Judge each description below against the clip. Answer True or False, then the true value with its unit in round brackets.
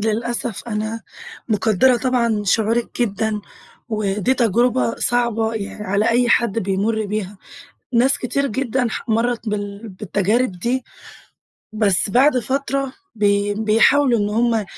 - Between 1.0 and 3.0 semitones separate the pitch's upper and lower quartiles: True (2.7 semitones)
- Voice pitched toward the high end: True (225 Hz)